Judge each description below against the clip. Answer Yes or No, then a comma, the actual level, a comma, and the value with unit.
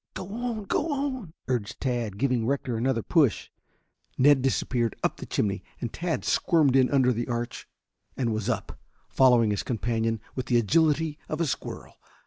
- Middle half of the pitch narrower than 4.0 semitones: No, average, 5.0 semitones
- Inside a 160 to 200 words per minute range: Yes, average, 165 wpm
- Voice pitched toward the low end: Yes, low, 130 Hz